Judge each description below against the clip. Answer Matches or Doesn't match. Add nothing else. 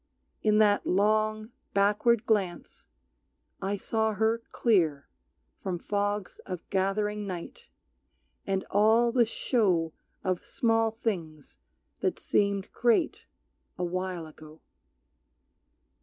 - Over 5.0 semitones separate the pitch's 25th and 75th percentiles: Doesn't match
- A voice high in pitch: Matches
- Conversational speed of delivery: Doesn't match